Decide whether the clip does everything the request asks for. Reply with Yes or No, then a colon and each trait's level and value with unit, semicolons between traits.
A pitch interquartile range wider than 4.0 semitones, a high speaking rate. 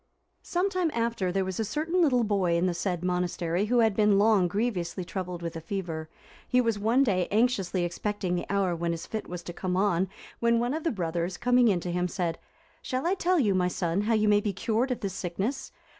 Yes: average, 4.7 semitones; fast, 230 wpm